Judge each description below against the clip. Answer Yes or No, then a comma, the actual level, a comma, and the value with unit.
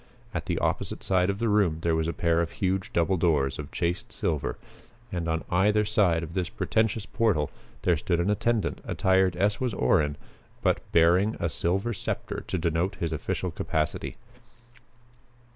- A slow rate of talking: No, average, 170 wpm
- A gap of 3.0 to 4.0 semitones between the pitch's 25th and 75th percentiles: Yes, average, 3.4 semitones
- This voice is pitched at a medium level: No, very low, 90 Hz